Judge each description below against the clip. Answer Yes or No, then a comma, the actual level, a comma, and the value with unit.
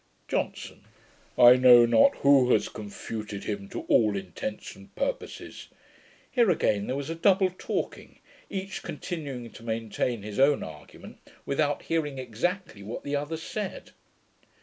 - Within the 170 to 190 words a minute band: No, average, 140 wpm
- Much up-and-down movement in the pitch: Yes, wide, 6.8 semitones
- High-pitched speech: No, low, 130 Hz